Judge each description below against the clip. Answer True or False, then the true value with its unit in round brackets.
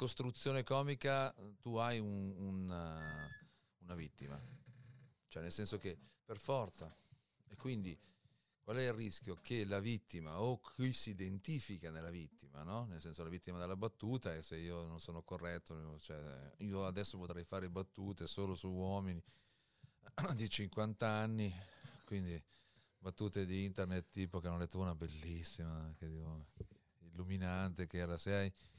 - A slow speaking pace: False (150 wpm)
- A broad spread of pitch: False (4.4 semitones)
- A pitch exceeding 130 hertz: False (95 Hz)